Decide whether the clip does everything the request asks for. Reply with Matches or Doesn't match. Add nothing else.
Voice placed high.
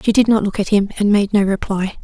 Matches